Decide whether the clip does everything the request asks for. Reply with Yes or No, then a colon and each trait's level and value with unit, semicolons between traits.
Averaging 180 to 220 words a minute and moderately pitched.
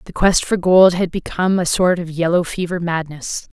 Yes: fast, 205 wpm; medium, 175 Hz